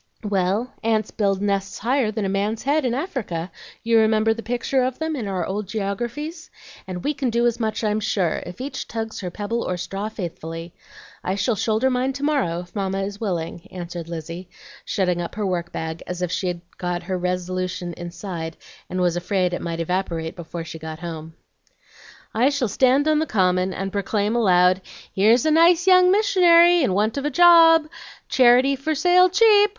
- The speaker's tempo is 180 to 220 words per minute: Yes, average, 190 wpm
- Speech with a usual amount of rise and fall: No, wide, 6.3 semitones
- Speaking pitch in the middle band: No, high, 205 Hz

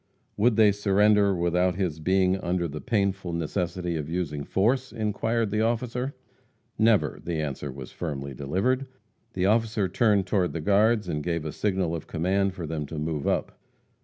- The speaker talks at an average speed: Yes, average, 165 wpm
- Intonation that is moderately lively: Yes, average, 4.4 semitones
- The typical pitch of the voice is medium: No, very low, 95 Hz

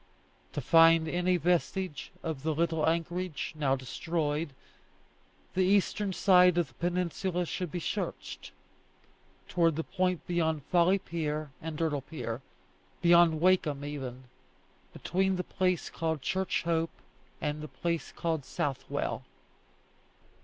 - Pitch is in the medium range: Yes, medium, 165 Hz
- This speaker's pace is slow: Yes, slow, 125 wpm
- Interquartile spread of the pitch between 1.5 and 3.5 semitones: Yes, average, 2.8 semitones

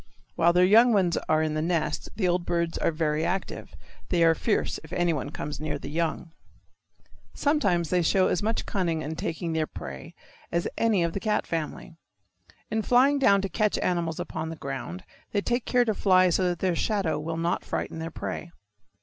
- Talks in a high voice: No, medium, 170 Hz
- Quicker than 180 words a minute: Yes, average, 195 wpm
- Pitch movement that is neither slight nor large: Yes, average, 3.5 semitones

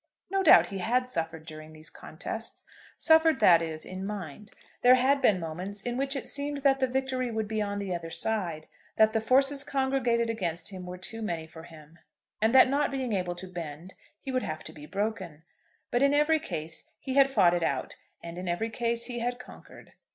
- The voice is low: No, high, 215 Hz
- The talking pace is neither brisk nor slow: No, fast, 210 wpm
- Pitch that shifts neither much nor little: No, wide, 7.1 semitones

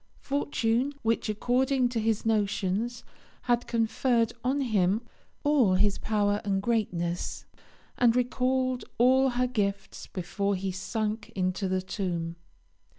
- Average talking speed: No, slow, 120 wpm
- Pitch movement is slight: No, average, 4.0 semitones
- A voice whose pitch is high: Yes, high, 225 Hz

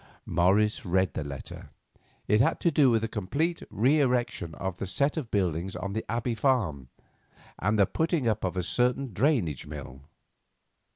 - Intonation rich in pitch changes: Yes, wide, 5.7 semitones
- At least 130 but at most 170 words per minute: Yes, average, 165 wpm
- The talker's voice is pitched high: No, low, 105 Hz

